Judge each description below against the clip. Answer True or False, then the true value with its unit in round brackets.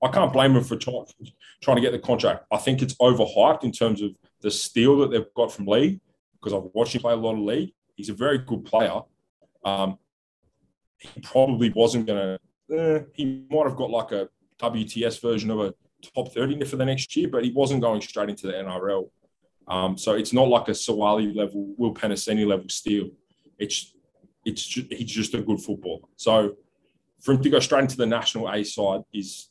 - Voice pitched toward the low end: True (115 Hz)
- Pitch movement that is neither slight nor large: True (4.1 semitones)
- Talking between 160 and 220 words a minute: True (205 wpm)